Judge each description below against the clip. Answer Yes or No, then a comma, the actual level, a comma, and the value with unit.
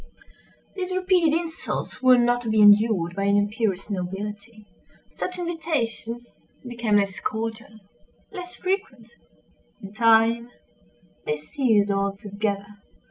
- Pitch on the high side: Yes, high, 225 Hz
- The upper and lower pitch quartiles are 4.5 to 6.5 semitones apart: No, average, 4.0 semitones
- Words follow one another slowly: Yes, slow, 100 wpm